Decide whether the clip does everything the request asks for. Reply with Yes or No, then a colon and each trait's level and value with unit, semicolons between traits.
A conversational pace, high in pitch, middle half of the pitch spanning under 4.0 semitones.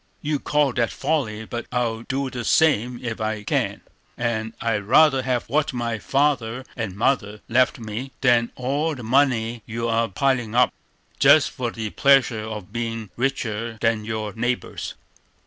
No: average, 160 wpm; low, 120 Hz; average, 2.9 semitones